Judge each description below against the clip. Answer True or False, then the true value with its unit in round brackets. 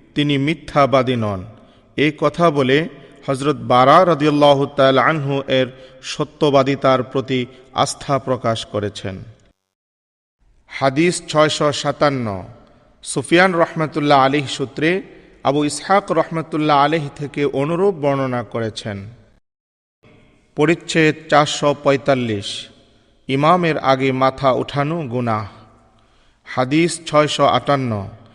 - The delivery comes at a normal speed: True (90 wpm)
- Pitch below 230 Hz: True (140 Hz)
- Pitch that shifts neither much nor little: True (3.9 semitones)